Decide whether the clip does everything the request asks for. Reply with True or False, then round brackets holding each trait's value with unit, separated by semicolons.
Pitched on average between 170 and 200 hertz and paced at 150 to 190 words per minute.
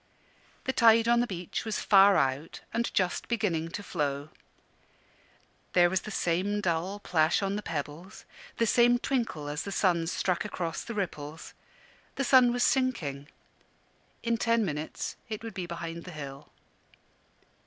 True (185 Hz; 155 wpm)